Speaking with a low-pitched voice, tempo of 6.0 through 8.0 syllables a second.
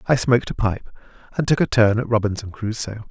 Yes: low, 115 Hz; 6.1 syllables/s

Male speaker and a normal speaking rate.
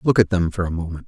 No: male; fast, 335 wpm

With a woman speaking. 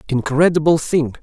No: male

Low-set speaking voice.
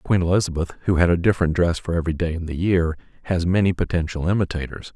Yes: very low, 85 Hz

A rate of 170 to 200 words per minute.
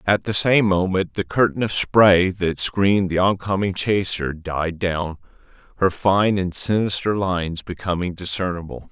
No: average, 155 wpm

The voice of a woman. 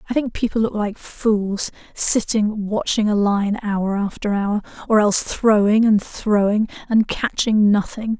Yes: female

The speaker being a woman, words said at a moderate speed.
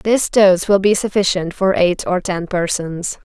Yes: female; average, 180 wpm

